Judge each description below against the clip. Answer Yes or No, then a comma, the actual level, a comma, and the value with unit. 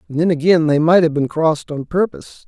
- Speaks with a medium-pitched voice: Yes, medium, 160 Hz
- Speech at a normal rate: No, fast, 240 wpm